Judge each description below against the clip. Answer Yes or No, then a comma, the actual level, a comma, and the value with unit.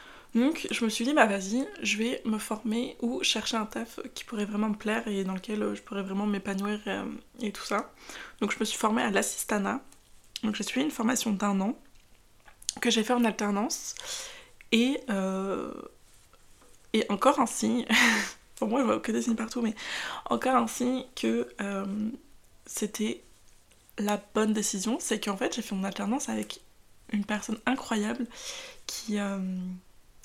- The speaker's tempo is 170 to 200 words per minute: Yes, average, 175 wpm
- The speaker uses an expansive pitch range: No, average, 3.3 semitones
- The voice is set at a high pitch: Yes, high, 220 Hz